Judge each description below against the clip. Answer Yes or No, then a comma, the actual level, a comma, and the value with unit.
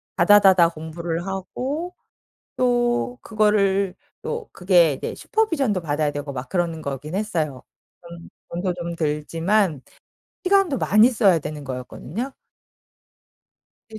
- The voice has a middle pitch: Yes, medium, 180 Hz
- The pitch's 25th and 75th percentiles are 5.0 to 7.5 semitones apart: Yes, wide, 5.4 semitones